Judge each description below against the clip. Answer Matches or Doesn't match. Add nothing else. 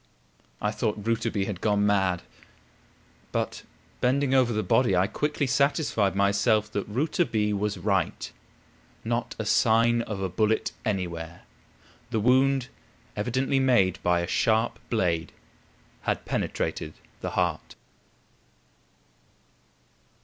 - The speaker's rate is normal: Doesn't match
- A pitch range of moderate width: Matches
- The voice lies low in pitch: Matches